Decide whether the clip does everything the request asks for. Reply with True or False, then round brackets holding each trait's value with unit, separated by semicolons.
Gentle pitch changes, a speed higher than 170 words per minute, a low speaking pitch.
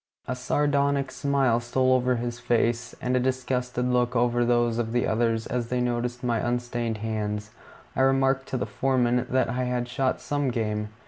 True (1.5 semitones; 180 wpm; 125 Hz)